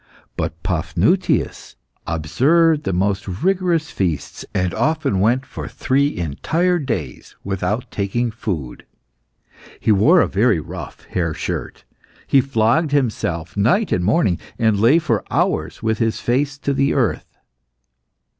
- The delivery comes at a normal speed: No, slow, 130 wpm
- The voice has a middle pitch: No, low, 115 Hz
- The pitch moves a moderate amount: No, wide, 7.1 semitones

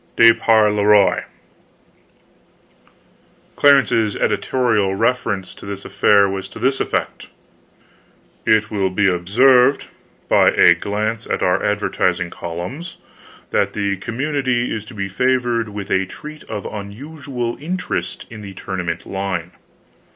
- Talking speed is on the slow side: Yes, slow, 130 wpm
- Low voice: Yes, low, 105 Hz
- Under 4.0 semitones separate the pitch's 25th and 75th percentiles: No, average, 4.3 semitones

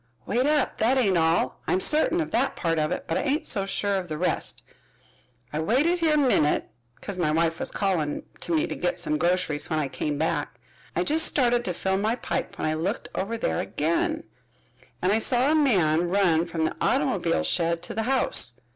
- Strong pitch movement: Yes, wide, 7.1 semitones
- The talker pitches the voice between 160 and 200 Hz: Yes, medium, 185 Hz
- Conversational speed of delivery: No, fast, 210 wpm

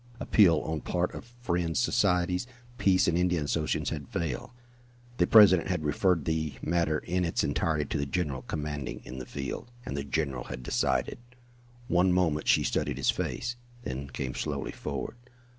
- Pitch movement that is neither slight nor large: Yes, average, 3.8 semitones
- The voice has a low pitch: Yes, very low, 80 Hz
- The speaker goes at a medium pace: Yes, average, 165 wpm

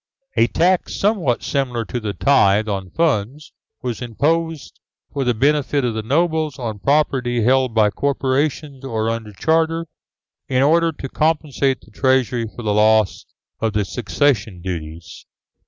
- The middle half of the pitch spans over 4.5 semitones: Yes, average, 5.2 semitones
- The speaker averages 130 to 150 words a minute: Yes, average, 145 wpm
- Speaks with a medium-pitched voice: No, low, 130 Hz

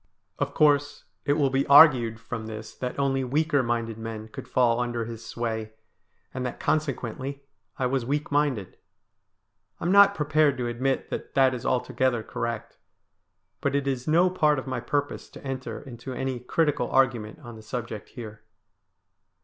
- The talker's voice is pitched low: Yes, low, 130 Hz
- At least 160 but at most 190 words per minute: Yes, average, 165 wpm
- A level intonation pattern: No, average, 3.3 semitones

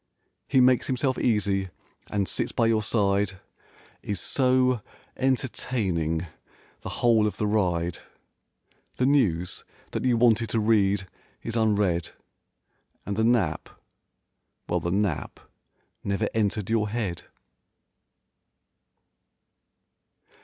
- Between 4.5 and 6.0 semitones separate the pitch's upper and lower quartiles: No, average, 3.5 semitones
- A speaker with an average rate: No, slow, 105 wpm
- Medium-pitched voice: No, low, 105 Hz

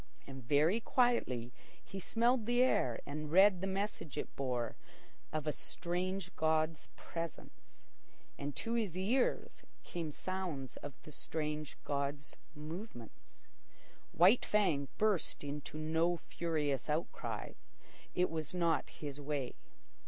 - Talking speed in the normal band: No, slow, 125 wpm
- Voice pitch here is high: No, medium, 160 Hz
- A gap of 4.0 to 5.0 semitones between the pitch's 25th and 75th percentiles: Yes, average, 4.7 semitones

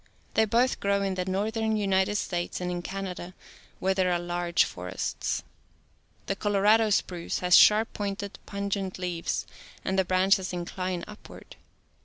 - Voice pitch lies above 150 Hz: Yes, high, 190 Hz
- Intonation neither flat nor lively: No, narrow, 2.1 semitones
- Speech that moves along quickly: No, average, 145 wpm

